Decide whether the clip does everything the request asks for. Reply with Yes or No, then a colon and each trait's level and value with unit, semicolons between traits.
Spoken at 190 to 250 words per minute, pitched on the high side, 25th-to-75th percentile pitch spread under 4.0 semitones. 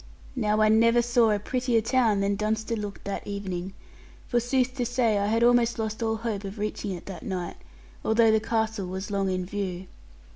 Yes: average, 195 wpm; high, 215 Hz; narrow, 2.6 semitones